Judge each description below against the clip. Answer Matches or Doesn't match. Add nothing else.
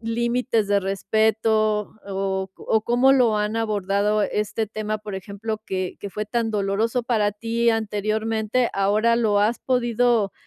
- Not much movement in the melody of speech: Matches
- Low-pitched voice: Doesn't match